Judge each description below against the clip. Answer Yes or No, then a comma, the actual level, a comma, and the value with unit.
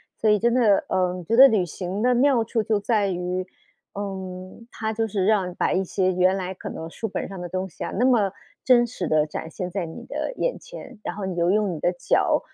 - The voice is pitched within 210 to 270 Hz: No, high, 195 Hz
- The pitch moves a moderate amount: Yes, average, 3.6 semitones